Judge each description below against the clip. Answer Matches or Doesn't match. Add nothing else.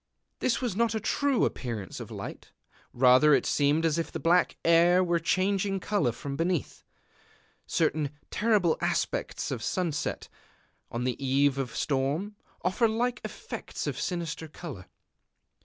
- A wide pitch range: Matches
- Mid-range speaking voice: Matches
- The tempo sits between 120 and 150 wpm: Matches